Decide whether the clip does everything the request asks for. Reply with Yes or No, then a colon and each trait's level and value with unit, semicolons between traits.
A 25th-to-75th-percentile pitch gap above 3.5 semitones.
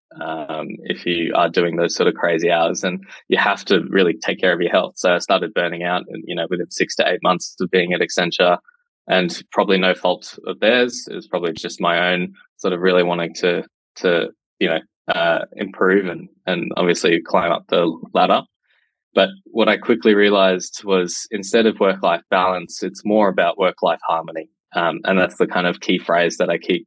No: average, 3.0 semitones